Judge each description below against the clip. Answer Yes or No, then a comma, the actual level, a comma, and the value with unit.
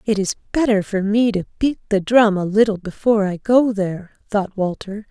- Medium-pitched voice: No, high, 205 Hz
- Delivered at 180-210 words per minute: Yes, average, 200 wpm